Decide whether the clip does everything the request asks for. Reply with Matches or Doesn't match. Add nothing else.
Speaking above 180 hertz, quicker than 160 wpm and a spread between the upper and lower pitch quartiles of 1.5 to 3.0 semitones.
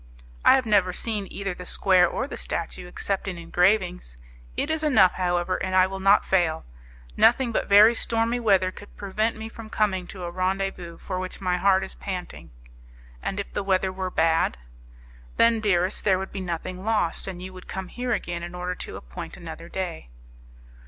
Matches